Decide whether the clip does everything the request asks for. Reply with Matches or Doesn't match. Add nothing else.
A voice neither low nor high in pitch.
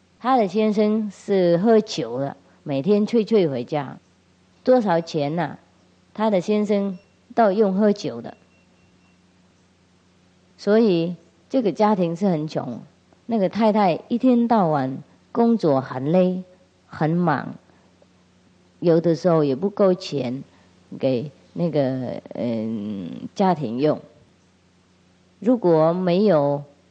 Matches